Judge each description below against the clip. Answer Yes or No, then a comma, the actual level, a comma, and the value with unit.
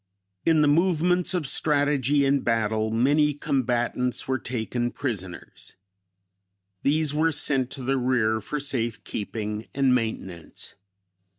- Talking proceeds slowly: Yes, slow, 120 wpm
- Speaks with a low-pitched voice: Yes, low, 130 Hz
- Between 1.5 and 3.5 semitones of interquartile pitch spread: No, average, 4.4 semitones